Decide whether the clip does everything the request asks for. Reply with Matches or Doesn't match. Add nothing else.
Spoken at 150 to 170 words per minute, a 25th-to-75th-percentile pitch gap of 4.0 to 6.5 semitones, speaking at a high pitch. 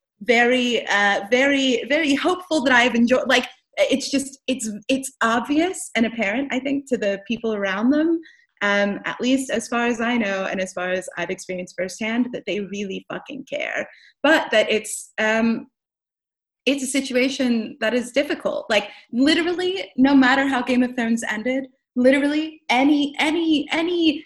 Matches